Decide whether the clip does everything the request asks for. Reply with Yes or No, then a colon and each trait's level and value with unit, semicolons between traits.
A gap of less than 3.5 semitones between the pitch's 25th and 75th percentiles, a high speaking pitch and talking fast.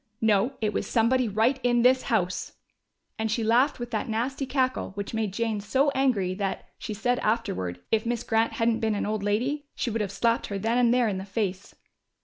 Yes: average, 3.1 semitones; high, 225 Hz; fast, 210 wpm